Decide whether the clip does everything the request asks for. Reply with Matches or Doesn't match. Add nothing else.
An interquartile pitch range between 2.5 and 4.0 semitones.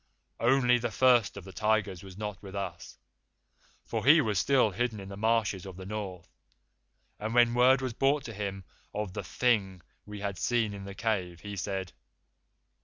Matches